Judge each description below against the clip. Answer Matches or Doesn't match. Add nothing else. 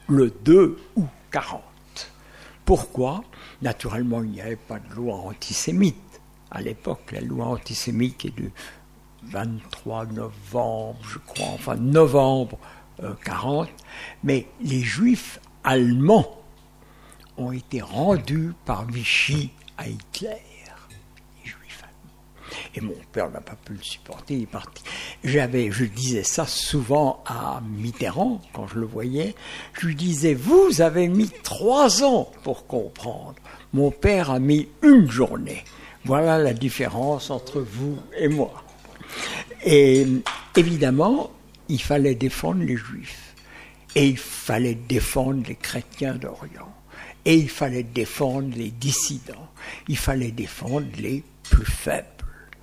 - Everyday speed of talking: Doesn't match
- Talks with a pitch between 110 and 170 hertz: Matches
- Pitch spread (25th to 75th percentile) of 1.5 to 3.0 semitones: Doesn't match